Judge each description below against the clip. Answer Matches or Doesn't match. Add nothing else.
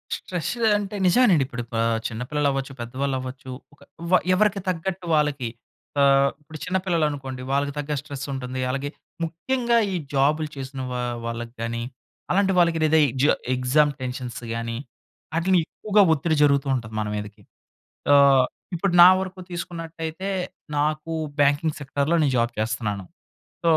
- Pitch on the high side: Doesn't match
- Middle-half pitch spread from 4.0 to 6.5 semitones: Matches